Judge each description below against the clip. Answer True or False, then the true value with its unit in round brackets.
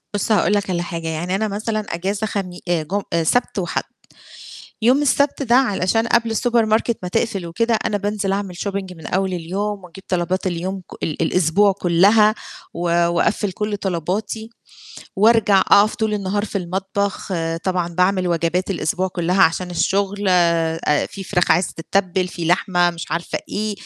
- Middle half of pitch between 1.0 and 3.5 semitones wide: True (3.0 semitones)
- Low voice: False (190 Hz)